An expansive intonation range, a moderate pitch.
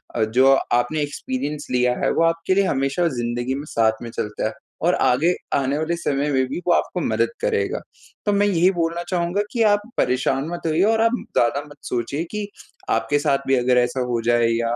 Yes: wide, 5.8 semitones; medium, 145 Hz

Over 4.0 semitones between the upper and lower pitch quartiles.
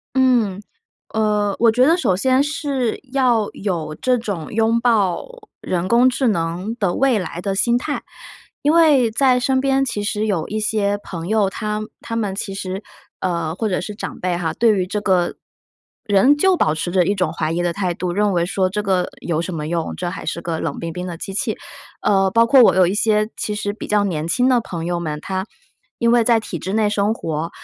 Yes: average, 4.6 semitones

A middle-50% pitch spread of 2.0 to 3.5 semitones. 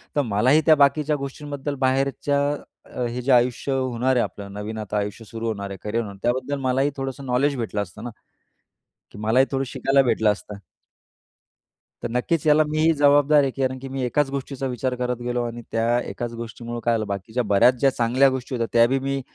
Yes: average, 3.0 semitones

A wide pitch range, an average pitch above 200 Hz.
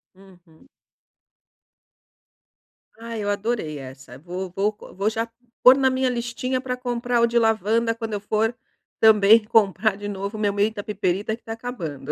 No: average, 3.1 semitones; high, 215 Hz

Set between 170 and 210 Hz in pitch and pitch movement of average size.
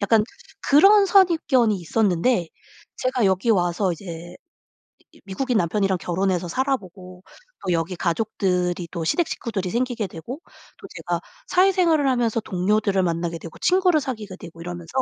No: high, 195 Hz; wide, 6.3 semitones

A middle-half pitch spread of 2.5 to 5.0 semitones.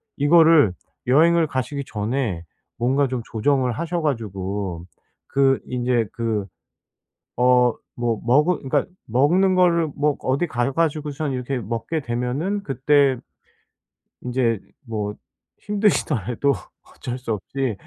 Yes: average, 4.3 semitones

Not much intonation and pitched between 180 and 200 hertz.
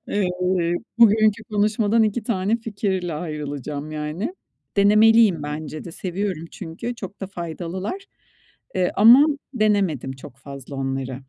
No: wide, 5.6 semitones; medium, 185 Hz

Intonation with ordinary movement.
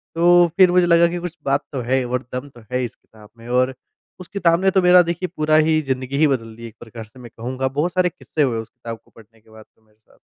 No: wide, 6.6 semitones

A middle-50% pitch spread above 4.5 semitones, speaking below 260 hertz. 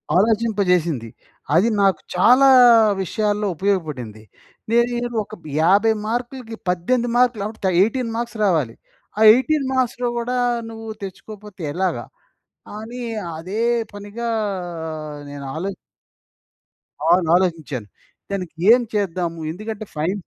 Yes: average, 4.9 semitones; high, 205 Hz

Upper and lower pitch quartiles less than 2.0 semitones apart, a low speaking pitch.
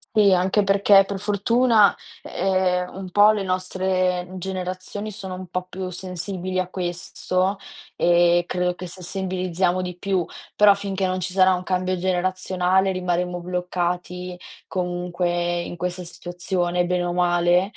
No: narrow, 1.2 semitones; medium, 185 Hz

